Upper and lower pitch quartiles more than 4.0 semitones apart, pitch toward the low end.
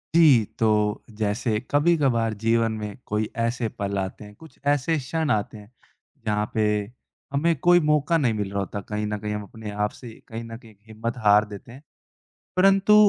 Yes: average, 5.0 semitones; low, 110 Hz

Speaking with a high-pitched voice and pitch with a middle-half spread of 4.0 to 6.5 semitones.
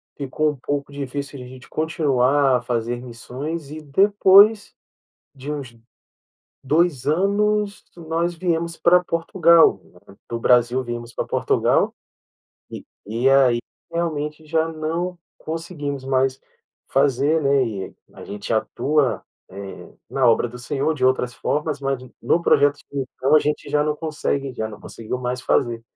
No: medium, 140 Hz; average, 4.3 semitones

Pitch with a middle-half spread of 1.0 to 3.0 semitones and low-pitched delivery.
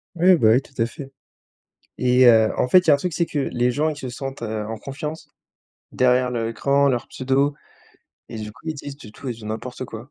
No: average, 3.5 semitones; low, 130 Hz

